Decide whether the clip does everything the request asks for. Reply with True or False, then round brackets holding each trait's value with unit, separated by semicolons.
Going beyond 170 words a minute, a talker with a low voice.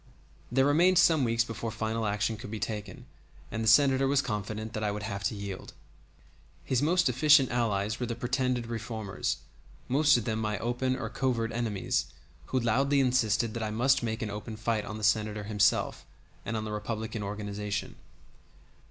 True (180 wpm; 115 Hz)